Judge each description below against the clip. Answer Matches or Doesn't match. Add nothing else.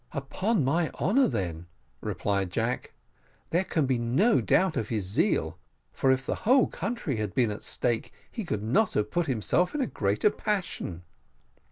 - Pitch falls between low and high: Doesn't match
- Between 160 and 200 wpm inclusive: Matches